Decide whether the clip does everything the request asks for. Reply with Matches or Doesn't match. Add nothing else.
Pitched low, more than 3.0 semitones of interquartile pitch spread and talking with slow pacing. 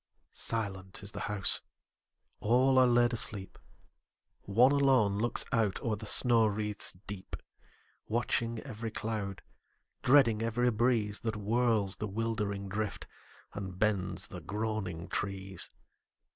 Doesn't match